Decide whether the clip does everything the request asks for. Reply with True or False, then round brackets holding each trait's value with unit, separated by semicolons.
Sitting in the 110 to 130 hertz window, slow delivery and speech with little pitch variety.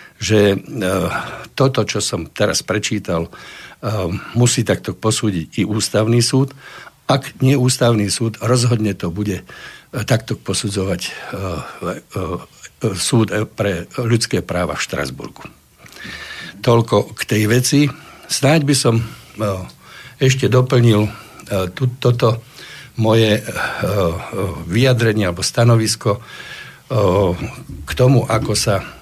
False (115 Hz; 95 wpm; 3.1 semitones)